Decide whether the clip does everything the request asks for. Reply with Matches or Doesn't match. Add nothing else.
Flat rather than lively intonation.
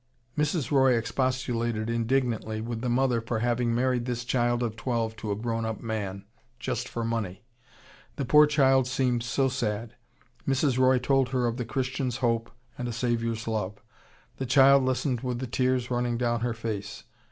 Matches